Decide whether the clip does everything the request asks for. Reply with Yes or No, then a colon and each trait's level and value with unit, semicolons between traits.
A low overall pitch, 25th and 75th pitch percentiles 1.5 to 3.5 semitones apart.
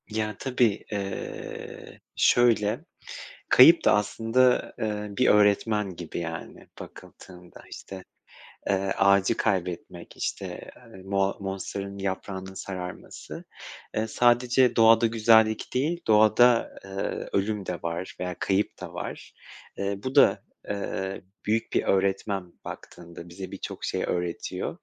Yes: low, 100 Hz; average, 2.9 semitones